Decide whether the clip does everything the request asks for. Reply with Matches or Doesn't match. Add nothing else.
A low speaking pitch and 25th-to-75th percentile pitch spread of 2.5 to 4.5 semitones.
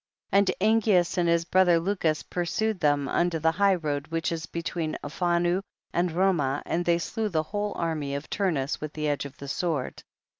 Doesn't match